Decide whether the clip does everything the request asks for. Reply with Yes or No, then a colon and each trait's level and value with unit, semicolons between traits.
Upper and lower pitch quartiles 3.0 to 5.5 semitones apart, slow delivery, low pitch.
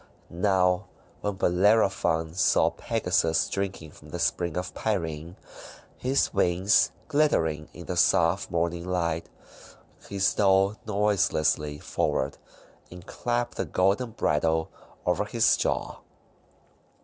Yes: average, 3.3 semitones; slow, 110 wpm; very low, 90 Hz